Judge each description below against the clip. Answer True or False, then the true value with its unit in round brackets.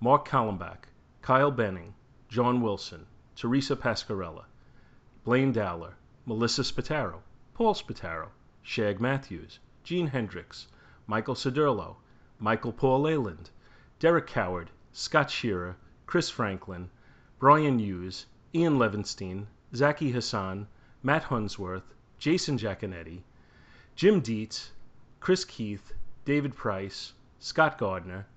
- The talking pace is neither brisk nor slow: False (100 wpm)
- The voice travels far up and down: True (5.8 semitones)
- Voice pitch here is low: True (115 Hz)